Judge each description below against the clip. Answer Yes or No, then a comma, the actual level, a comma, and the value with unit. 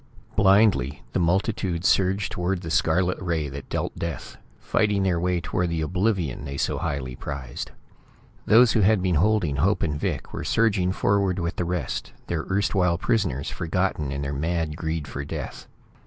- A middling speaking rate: Yes, average, 170 wpm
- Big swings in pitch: No, average, 4.0 semitones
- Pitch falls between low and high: No, very low, 85 Hz